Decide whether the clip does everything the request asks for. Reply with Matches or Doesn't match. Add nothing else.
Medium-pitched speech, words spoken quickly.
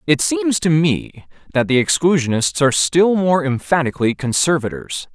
Doesn't match